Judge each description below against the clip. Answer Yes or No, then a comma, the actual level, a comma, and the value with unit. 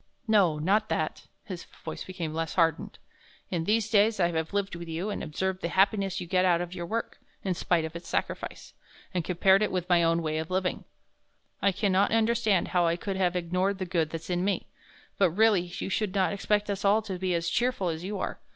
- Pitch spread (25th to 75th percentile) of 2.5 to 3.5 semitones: Yes, average, 2.8 semitones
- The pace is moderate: No, fast, 225 wpm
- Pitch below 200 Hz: Yes, medium, 185 Hz